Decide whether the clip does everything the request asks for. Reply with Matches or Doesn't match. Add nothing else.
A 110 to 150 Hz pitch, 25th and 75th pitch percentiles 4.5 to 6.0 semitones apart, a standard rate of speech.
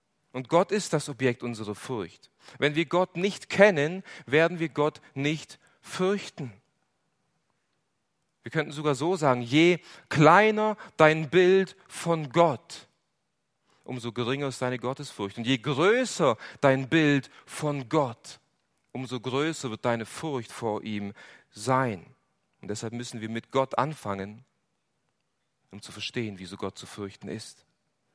Matches